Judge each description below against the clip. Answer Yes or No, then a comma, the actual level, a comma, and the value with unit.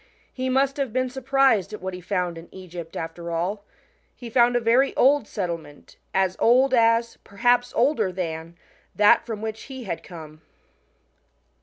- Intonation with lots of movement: Yes, wide, 6.0 semitones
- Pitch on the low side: No, high, 215 Hz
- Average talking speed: Yes, average, 165 wpm